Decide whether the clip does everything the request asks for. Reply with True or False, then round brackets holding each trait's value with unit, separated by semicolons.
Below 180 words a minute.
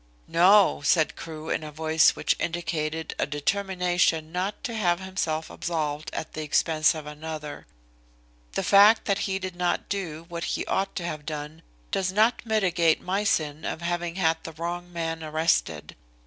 True (165 wpm)